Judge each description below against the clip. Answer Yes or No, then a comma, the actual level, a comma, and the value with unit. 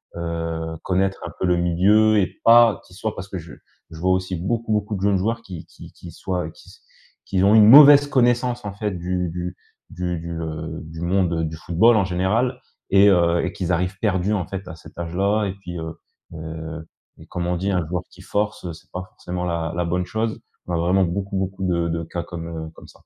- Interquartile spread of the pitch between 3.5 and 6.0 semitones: No, average, 3.1 semitones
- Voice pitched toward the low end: Yes, very low, 90 Hz